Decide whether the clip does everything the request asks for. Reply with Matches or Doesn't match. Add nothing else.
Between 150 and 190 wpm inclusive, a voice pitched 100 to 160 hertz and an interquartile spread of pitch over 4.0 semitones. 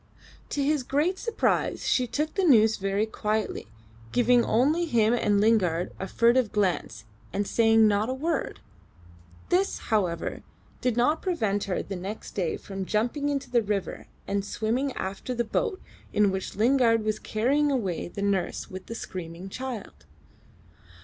Doesn't match